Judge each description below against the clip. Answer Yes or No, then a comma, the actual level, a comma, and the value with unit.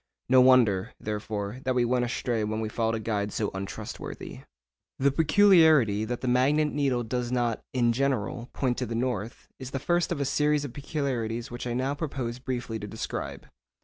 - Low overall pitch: Yes, low, 125 Hz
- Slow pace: No, average, 185 wpm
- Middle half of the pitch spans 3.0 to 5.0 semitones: Yes, average, 3.5 semitones